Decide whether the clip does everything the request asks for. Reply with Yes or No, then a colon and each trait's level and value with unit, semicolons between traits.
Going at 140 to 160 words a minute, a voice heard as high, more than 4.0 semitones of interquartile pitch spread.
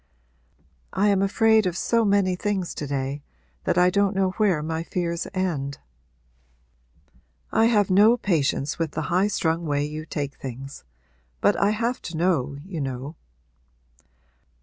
No: average, 145 wpm; medium, 180 Hz; average, 5.3 semitones